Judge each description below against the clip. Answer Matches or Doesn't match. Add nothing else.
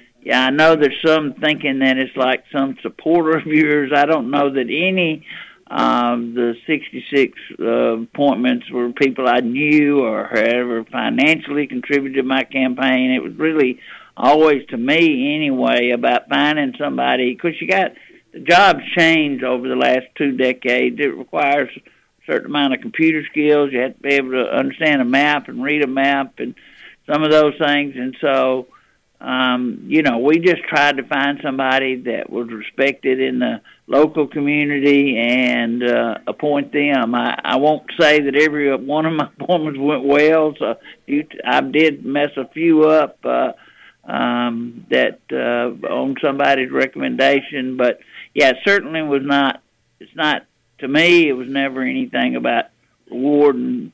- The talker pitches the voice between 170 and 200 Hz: Doesn't match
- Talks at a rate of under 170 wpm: Matches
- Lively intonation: Doesn't match